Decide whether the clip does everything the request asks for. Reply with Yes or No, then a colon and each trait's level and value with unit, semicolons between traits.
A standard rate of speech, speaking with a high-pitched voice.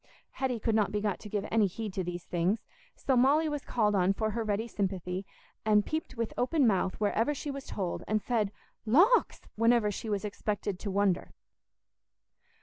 Yes: average, 185 wpm; high, 215 Hz